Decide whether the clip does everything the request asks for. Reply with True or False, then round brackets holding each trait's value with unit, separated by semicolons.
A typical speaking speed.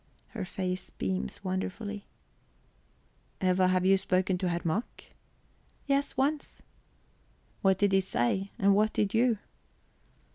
False (120 wpm)